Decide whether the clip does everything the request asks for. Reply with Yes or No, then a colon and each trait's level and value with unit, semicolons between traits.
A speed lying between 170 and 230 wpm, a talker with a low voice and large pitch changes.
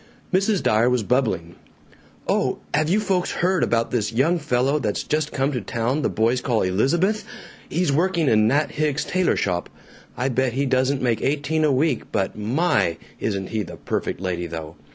Yes: average, 185 wpm; low, 130 Hz; wide, 6.1 semitones